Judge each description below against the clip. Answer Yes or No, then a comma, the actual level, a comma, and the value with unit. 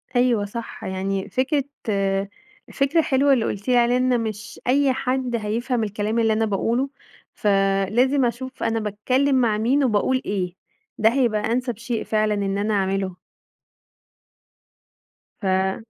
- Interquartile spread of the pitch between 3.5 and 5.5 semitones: Yes, average, 3.9 semitones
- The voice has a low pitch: No, high, 225 Hz